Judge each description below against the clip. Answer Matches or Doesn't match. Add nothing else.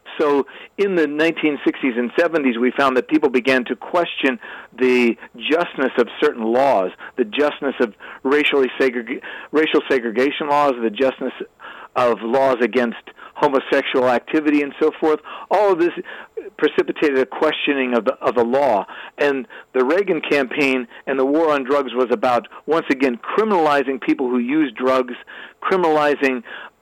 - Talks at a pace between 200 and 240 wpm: Doesn't match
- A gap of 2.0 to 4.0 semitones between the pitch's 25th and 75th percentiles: Matches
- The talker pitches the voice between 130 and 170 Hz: Matches